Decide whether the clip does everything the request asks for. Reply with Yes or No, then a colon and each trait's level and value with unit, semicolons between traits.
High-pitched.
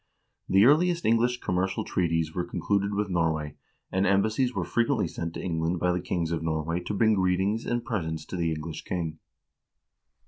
No: very low, 90 Hz